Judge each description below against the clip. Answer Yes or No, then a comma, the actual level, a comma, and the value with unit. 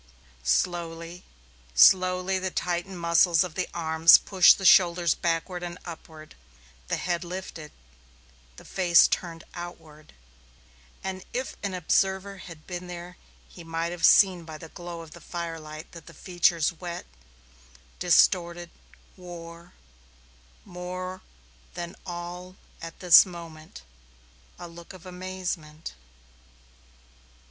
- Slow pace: Yes, slow, 120 wpm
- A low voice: No, medium, 175 Hz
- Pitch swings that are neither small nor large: No, narrow, 1.6 semitones